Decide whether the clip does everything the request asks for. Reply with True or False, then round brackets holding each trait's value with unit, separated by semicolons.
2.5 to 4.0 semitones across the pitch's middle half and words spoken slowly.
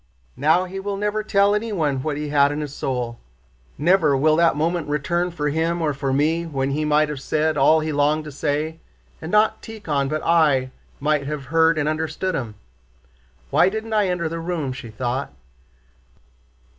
False (3.1 semitones; 180 wpm)